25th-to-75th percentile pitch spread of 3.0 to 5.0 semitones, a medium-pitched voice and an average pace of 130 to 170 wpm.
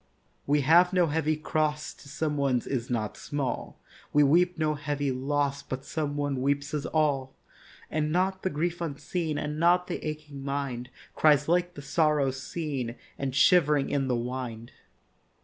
No: narrow, 2.4 semitones; medium, 145 Hz; average, 165 wpm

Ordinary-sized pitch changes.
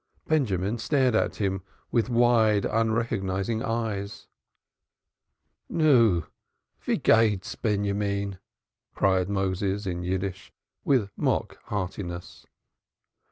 Yes: average, 3.0 semitones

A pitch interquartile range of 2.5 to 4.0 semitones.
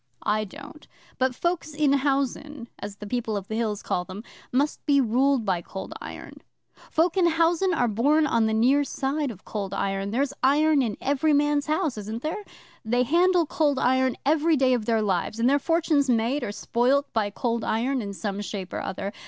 No: average, 5.2 semitones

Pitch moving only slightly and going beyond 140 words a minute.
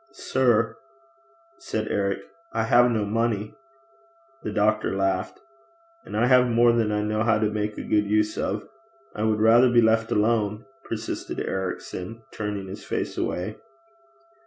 Yes: narrow, 1.6 semitones; average, 150 wpm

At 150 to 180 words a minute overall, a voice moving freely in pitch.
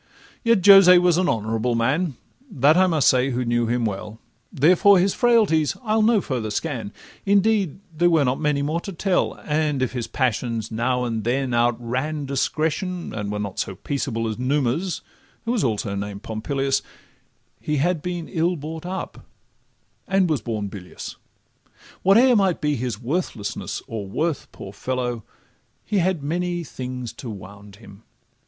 Yes: average, 160 wpm; wide, 7.3 semitones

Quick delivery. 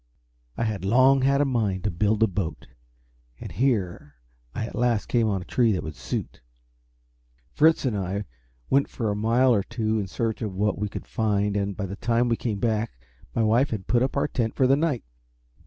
Yes: fast, 210 wpm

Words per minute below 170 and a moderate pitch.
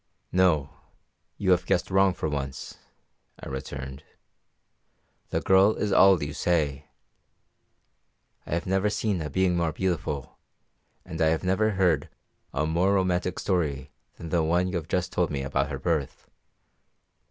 No: average, 150 wpm; very low, 85 Hz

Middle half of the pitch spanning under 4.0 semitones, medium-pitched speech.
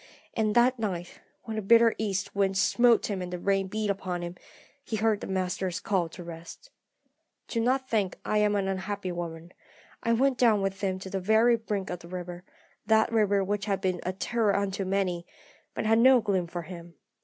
No: average, 3.1 semitones; high, 195 Hz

